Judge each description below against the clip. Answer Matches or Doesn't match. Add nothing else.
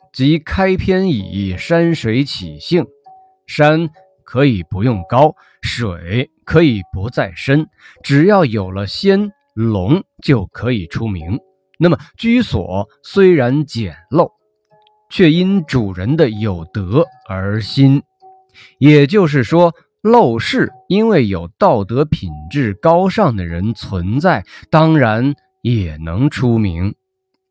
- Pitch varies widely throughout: Matches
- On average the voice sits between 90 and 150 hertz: Matches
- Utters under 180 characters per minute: Matches